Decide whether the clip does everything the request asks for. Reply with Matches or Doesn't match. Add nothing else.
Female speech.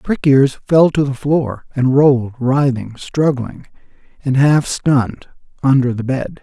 Doesn't match